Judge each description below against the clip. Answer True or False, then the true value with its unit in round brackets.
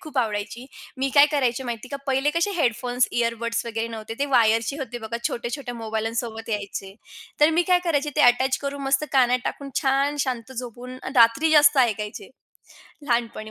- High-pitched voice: True (245 Hz)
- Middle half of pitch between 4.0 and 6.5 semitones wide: False (3.4 semitones)